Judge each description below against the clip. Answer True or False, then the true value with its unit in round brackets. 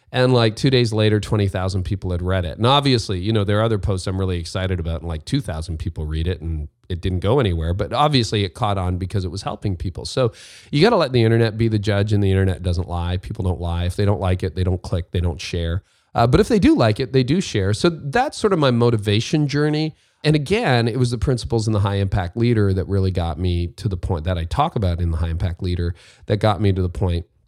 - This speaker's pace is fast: True (265 wpm)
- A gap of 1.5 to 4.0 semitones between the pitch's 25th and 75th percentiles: False (4.5 semitones)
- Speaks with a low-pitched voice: True (100 Hz)